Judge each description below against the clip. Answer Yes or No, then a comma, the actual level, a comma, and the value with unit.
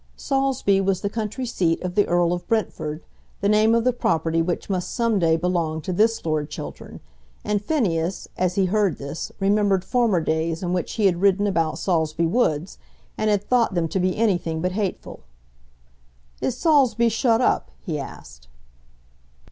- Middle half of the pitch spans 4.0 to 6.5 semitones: Yes, average, 4.6 semitones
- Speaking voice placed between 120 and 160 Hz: No, high, 190 Hz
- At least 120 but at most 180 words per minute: Yes, average, 170 wpm